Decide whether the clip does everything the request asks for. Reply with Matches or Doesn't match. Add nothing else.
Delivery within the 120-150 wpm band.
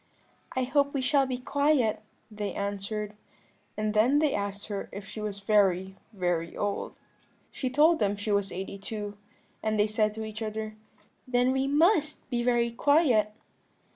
Doesn't match